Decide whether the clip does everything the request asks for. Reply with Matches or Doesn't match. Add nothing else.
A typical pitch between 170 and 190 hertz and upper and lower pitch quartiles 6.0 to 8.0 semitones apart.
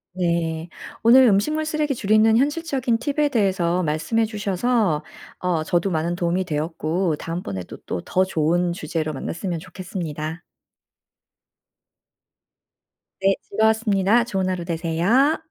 Doesn't match